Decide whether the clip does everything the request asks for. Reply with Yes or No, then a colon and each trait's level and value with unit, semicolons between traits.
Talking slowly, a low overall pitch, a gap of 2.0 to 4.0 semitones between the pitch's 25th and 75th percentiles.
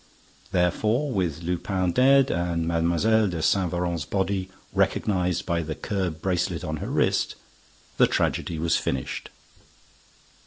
Yes: slow, 125 wpm; very low, 90 Hz; average, 2.7 semitones